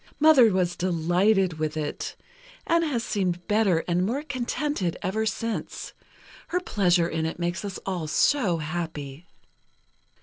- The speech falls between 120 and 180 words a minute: Yes, slow, 135 wpm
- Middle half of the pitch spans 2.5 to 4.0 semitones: No, average, 4.8 semitones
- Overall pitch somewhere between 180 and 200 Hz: Yes, medium, 185 Hz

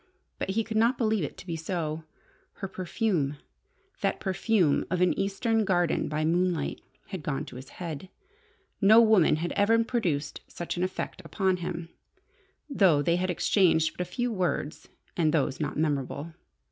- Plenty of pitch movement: No, average, 4.2 semitones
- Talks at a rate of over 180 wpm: No, average, 165 wpm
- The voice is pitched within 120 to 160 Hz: No, medium, 180 Hz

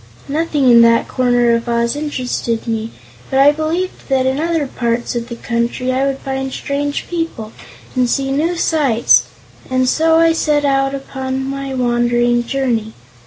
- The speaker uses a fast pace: No, average, 165 wpm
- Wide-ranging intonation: No, average, 3.2 semitones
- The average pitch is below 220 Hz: No, very high, 265 Hz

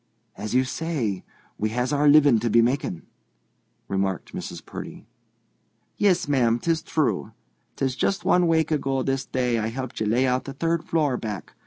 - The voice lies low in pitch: Yes, low, 130 Hz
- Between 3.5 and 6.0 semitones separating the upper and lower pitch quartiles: Yes, average, 4.6 semitones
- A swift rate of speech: No, average, 170 wpm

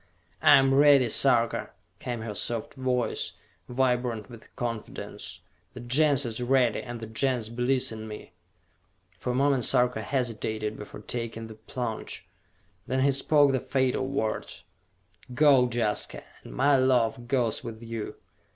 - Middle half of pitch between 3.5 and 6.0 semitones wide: No, average, 2.8 semitones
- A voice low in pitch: Yes, low, 120 Hz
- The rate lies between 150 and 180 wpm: No, average, 140 wpm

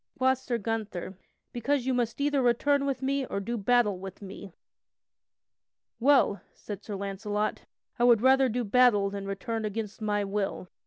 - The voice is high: Yes, high, 225 Hz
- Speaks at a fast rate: No, average, 160 wpm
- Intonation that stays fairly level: No, average, 4.1 semitones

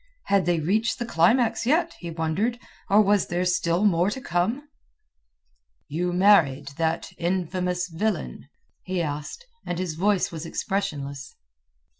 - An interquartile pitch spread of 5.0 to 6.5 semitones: No, average, 4.0 semitones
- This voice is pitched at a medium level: Yes, medium, 180 Hz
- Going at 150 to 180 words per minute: No, slow, 135 wpm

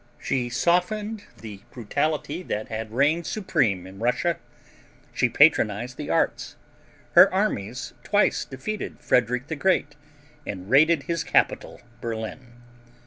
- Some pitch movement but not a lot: No, wide, 6.9 semitones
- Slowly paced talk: Yes, slow, 120 wpm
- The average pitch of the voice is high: No, low, 130 Hz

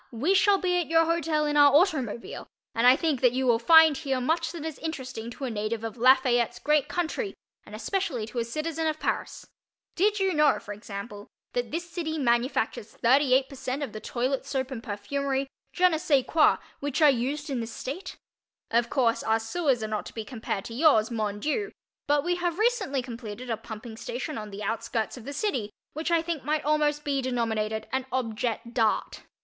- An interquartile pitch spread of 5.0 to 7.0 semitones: Yes, average, 5.3 semitones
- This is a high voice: Yes, very high, 265 Hz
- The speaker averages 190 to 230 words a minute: Yes, average, 200 wpm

